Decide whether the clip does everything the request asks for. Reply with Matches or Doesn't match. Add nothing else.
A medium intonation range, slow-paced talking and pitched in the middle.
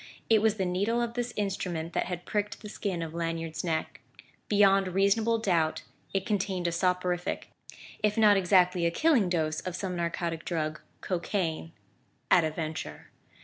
Doesn't match